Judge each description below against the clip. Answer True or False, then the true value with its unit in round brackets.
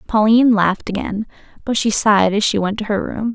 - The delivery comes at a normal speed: False (215 wpm)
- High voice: True (210 Hz)